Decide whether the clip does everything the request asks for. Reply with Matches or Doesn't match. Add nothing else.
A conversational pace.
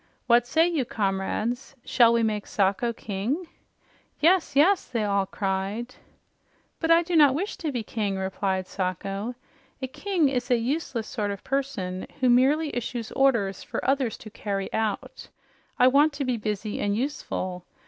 Matches